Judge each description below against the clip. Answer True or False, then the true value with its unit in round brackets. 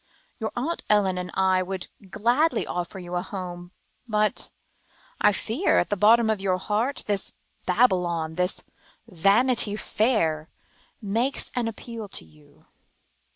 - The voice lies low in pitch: False (205 Hz)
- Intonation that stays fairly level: False (3.9 semitones)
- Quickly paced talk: False (140 wpm)